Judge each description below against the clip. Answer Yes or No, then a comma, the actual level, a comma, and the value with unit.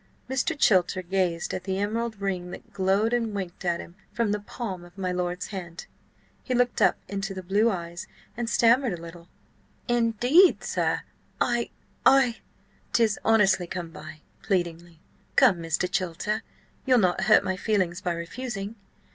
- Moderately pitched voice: No, high, 195 Hz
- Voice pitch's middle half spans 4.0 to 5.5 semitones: Yes, average, 4.5 semitones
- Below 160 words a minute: Yes, average, 150 wpm